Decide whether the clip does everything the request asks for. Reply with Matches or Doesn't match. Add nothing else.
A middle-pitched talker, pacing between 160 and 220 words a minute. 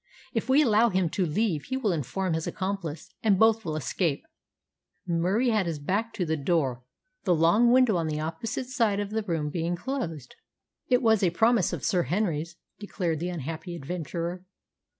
Matches